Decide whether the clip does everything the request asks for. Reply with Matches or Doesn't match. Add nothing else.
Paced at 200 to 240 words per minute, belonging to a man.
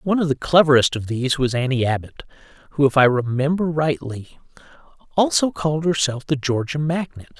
Doesn't match